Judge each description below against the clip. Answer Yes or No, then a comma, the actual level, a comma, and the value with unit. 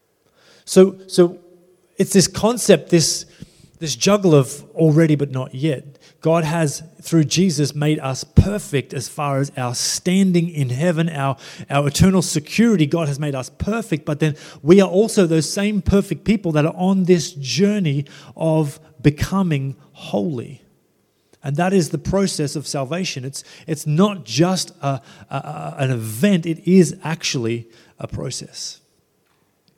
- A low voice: No, medium, 160 Hz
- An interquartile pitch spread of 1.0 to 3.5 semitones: No, average, 4.1 semitones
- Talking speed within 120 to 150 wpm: Yes, average, 145 wpm